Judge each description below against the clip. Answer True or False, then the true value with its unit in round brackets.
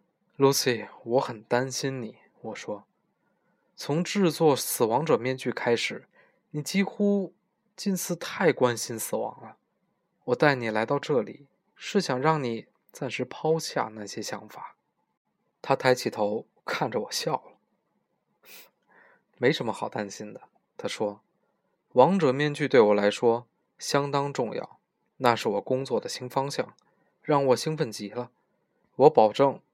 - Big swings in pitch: False (4.5 semitones)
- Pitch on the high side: False (140 Hz)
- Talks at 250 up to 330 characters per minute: False (200 characters per minute)